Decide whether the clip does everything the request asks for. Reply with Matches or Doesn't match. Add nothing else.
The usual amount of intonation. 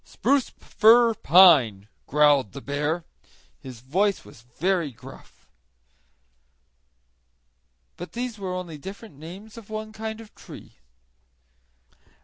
Doesn't match